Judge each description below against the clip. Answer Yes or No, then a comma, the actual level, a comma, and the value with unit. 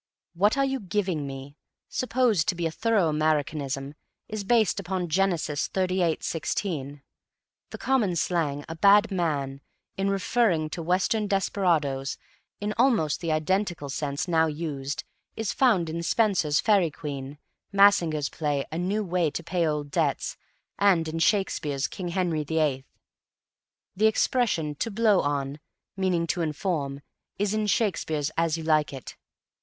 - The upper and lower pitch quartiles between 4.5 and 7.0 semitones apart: Yes, average, 4.8 semitones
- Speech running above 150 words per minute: No, average, 140 wpm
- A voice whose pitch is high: No, medium, 170 Hz